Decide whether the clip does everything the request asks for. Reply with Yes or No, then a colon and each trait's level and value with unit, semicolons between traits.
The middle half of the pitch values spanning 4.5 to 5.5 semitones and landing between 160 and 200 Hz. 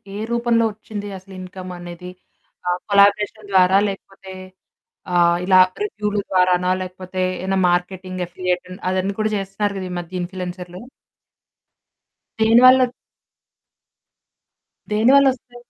No: narrow, 2.5 semitones; high, 190 Hz